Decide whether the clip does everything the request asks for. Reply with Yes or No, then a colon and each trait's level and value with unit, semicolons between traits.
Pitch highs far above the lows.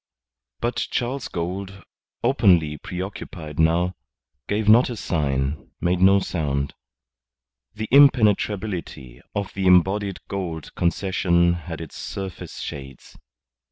No: average, 3.8 semitones